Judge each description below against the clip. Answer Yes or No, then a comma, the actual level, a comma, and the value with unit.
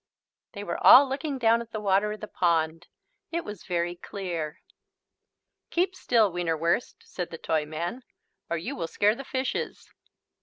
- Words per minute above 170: No, average, 155 wpm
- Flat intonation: No, wide, 5.6 semitones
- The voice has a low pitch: No, high, 195 Hz